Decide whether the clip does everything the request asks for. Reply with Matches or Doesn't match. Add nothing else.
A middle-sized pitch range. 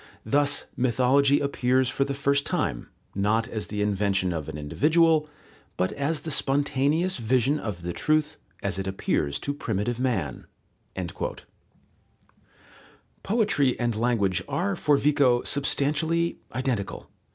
Doesn't match